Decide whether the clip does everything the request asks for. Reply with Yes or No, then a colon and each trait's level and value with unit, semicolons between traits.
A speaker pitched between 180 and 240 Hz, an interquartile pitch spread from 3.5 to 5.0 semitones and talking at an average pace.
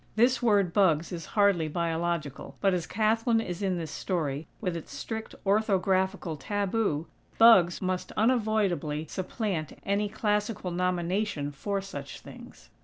No: high, 190 Hz; average, 3.8 semitones; slow, 130 wpm